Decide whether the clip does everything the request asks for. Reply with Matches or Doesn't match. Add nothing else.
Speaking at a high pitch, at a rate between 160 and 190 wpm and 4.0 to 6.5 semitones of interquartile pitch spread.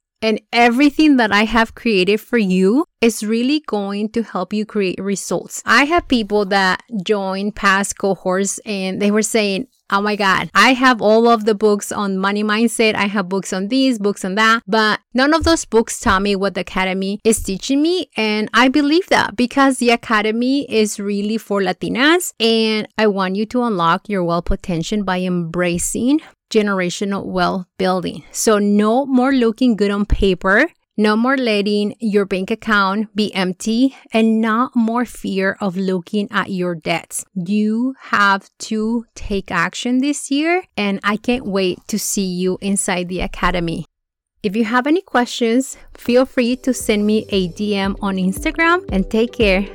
Doesn't match